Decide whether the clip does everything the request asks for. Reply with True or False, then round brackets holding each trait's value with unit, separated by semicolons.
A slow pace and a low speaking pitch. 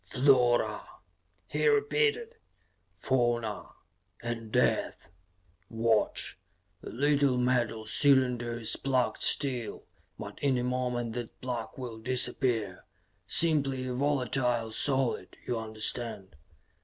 True (100 wpm; 125 Hz)